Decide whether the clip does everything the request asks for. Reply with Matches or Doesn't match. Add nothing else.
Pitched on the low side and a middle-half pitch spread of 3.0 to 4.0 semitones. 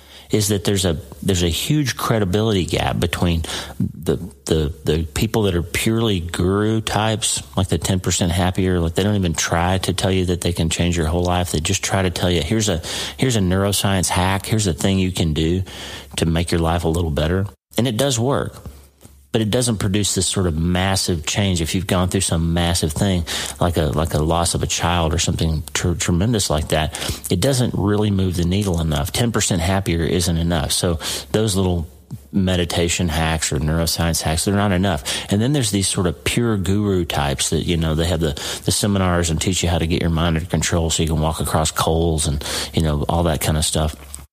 Matches